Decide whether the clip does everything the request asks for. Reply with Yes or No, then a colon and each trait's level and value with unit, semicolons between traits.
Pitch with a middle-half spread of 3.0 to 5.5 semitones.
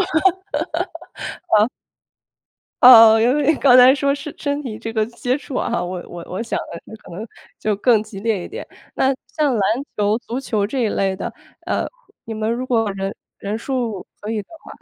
Yes: average, 4.1 semitones